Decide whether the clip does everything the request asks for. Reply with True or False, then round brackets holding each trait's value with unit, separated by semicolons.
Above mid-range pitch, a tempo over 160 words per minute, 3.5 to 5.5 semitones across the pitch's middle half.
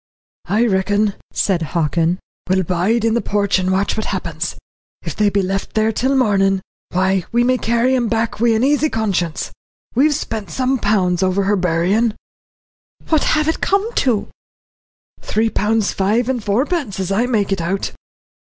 True (210 Hz; 170 wpm; 3.8 semitones)